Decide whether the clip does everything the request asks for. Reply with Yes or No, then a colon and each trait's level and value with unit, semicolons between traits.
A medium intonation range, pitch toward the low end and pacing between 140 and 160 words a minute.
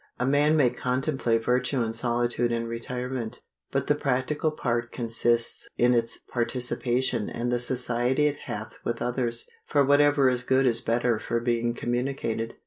No: narrow, 1.8 semitones; low, 120 Hz; average, 155 wpm